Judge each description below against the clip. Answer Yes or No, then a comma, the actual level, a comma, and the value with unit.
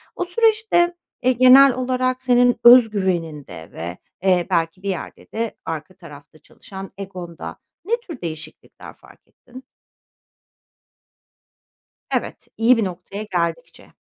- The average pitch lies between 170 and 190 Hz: No, high, 200 Hz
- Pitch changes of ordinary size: No, wide, 7.1 semitones